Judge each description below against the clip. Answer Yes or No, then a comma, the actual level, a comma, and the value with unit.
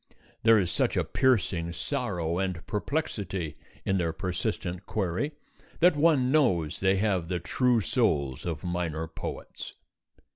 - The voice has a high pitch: No, very low, 95 Hz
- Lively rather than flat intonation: Yes, wide, 6.2 semitones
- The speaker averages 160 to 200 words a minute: No, slow, 135 wpm